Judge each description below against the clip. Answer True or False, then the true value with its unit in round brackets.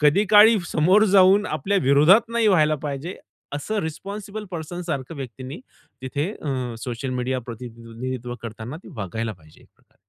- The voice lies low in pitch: False (145 Hz)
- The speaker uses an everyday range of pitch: False (7.6 semitones)